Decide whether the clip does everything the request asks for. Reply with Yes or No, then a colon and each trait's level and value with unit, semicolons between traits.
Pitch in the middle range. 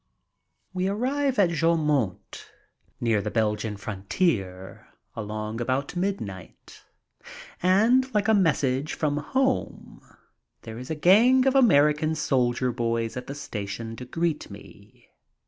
Yes: medium, 145 Hz